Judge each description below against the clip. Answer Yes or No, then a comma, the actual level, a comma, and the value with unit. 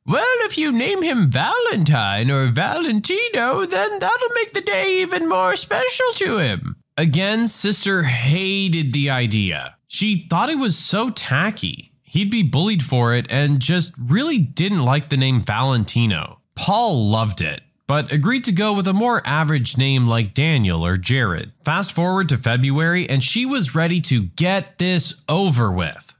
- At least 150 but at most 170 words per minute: Yes, average, 165 wpm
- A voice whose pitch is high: No, medium, 160 Hz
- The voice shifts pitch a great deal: Yes, wide, 8.0 semitones